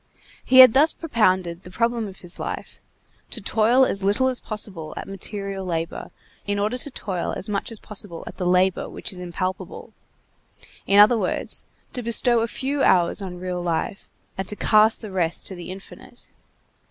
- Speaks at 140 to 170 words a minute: No, average, 180 wpm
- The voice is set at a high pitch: Yes, high, 200 Hz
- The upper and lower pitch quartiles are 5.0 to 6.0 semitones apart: No, average, 3.8 semitones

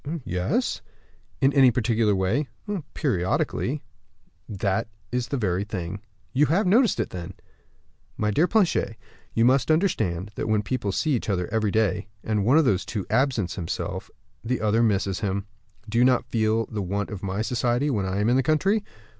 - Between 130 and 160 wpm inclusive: No, average, 170 wpm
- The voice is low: Yes, low, 110 Hz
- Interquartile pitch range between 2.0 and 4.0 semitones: No, average, 4.7 semitones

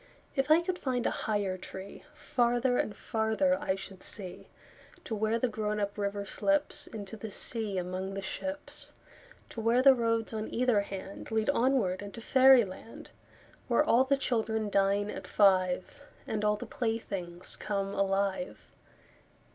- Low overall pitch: No, high, 215 Hz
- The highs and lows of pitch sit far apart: No, average, 3.8 semitones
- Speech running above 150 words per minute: No, slow, 135 wpm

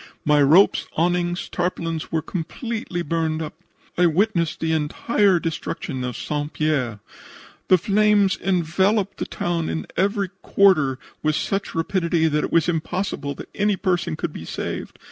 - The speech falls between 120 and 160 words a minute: Yes, average, 145 wpm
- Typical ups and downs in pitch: Yes, average, 3.6 semitones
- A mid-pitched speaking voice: Yes, medium, 170 Hz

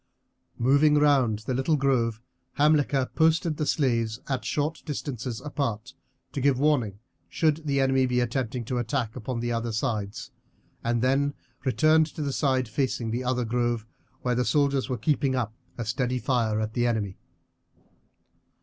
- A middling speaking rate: Yes, average, 160 wpm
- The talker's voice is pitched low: Yes, low, 130 Hz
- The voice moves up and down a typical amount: Yes, average, 3.3 semitones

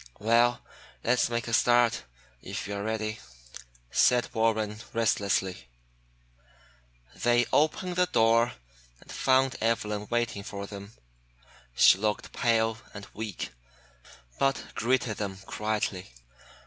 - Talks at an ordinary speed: No, slow, 110 wpm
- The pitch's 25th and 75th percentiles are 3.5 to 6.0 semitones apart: No, narrow, 2.4 semitones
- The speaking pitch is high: No, low, 115 Hz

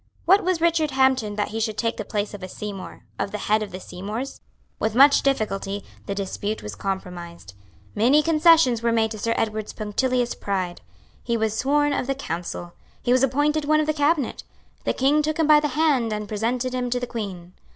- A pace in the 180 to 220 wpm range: Yes, fast, 205 wpm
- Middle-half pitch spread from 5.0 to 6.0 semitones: Yes, wide, 5.5 semitones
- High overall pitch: Yes, high, 230 Hz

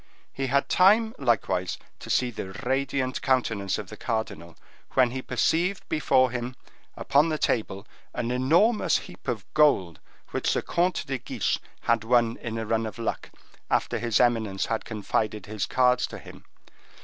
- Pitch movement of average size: Yes, average, 3.7 semitones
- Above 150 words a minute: Yes, average, 160 wpm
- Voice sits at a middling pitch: No, low, 120 Hz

